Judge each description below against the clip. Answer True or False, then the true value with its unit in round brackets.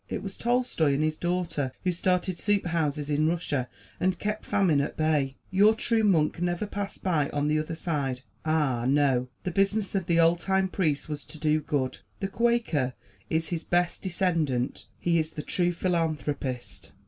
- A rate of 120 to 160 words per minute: False (180 wpm)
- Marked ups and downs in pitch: False (4.0 semitones)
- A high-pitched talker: False (165 Hz)